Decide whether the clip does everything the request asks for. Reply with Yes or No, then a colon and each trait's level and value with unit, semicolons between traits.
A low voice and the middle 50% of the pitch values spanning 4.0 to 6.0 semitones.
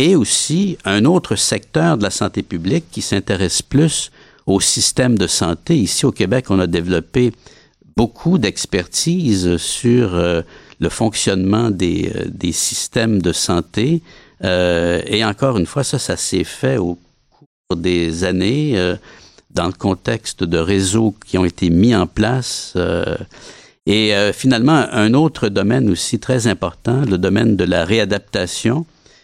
Yes: low, 100 Hz; average, 5.3 semitones